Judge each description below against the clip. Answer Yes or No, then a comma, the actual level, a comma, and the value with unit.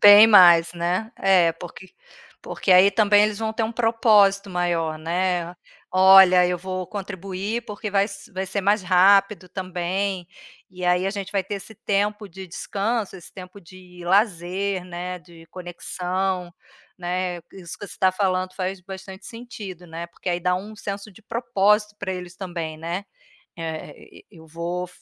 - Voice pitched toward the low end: No, medium, 185 Hz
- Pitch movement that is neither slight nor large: No, narrow, 2.1 semitones